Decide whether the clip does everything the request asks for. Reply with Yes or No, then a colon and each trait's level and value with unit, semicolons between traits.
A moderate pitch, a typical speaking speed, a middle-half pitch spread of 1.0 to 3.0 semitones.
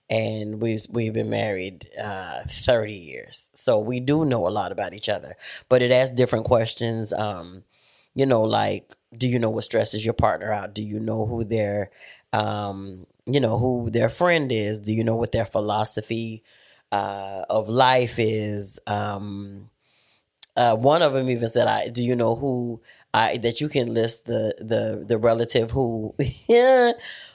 No: low, 115 Hz; average, 170 wpm; narrow, 2.6 semitones